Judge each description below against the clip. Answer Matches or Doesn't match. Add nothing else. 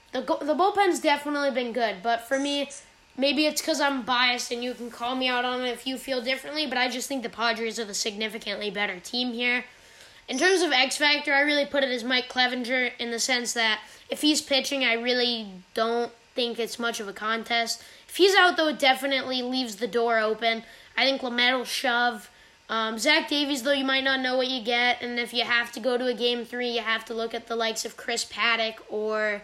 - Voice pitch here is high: Matches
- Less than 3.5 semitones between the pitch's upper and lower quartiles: Matches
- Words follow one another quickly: Matches